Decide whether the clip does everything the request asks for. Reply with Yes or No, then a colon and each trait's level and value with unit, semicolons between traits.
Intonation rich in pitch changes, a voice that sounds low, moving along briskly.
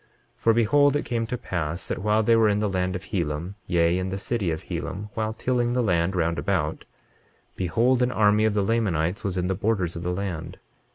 No: average, 4.2 semitones; low, 100 Hz; fast, 225 wpm